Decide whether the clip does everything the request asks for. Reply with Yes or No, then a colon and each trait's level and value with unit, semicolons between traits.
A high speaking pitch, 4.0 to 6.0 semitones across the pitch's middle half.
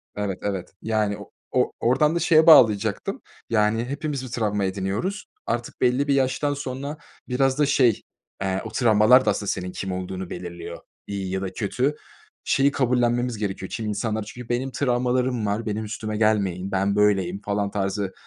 No: low, 110 Hz; average, 4.4 semitones